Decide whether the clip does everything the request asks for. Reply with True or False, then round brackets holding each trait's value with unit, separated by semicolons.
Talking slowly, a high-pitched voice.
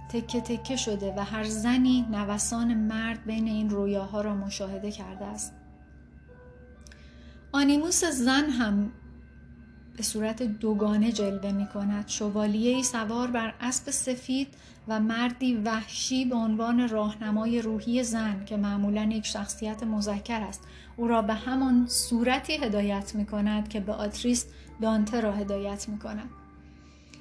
False (130 wpm; 215 Hz)